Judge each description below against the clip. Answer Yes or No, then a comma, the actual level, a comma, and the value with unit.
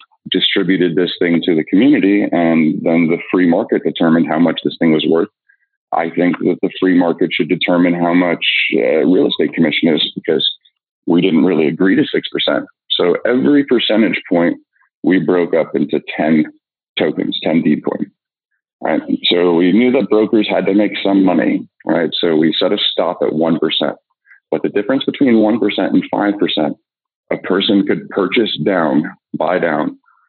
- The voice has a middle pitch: No, low, 105 Hz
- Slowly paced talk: No, average, 170 wpm